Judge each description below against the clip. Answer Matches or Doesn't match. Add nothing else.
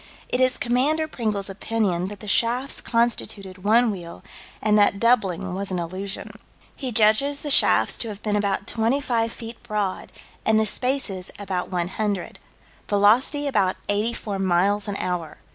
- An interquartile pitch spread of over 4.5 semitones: Doesn't match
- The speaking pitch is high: Matches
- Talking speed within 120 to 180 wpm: Matches